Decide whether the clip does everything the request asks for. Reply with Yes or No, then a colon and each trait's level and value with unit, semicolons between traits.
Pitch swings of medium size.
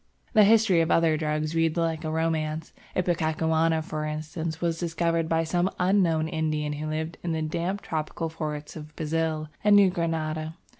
No: narrow, 1.3 semitones